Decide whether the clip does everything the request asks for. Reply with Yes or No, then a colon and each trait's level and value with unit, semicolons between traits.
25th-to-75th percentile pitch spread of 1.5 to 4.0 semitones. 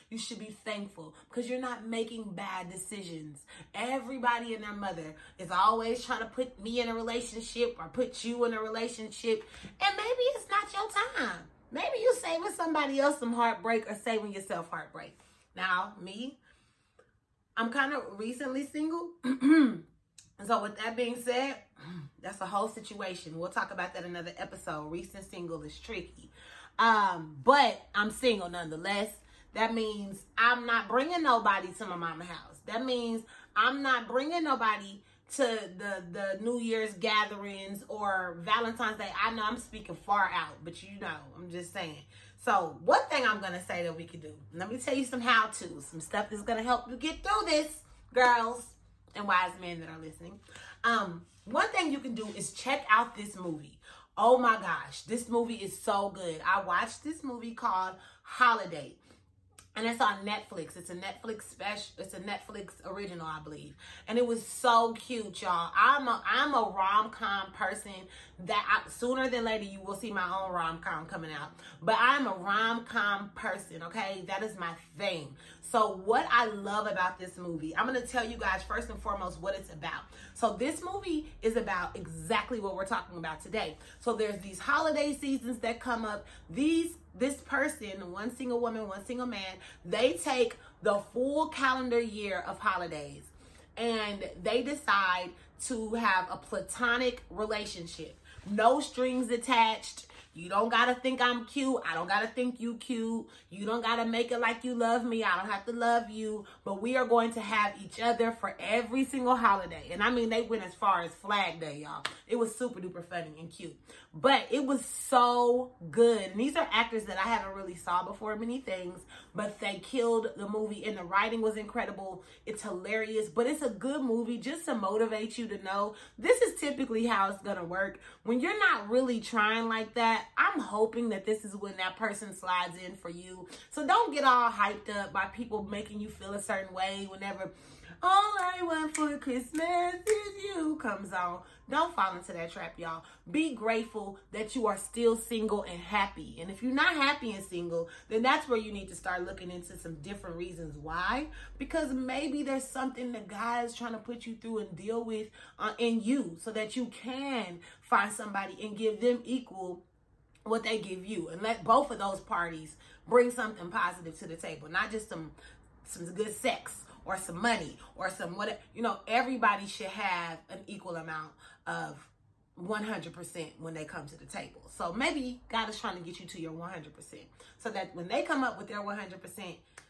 No: average, 4.4 semitones